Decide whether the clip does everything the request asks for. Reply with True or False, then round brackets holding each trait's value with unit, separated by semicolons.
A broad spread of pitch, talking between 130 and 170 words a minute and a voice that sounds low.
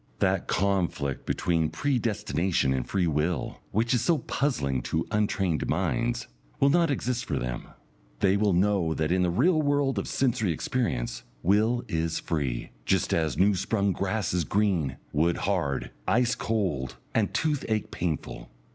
True (6.3 semitones; 150 wpm; 95 Hz)